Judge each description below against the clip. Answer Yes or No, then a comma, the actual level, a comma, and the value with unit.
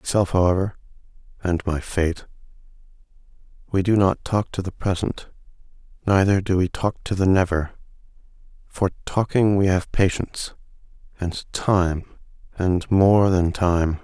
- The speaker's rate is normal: No, slow, 125 wpm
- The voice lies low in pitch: Yes, very low, 95 Hz